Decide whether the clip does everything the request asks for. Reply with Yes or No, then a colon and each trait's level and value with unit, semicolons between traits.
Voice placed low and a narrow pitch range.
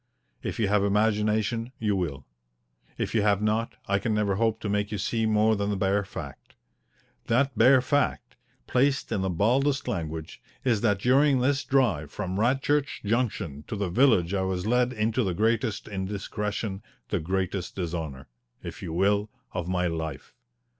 No: low, 105 Hz; average, 3.5 semitones